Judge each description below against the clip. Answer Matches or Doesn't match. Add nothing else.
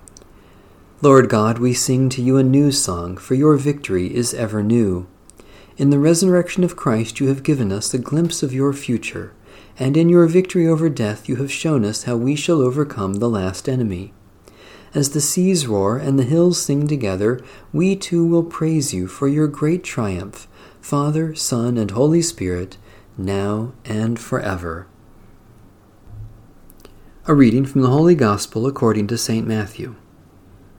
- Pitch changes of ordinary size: Doesn't match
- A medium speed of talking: Matches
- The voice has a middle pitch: Doesn't match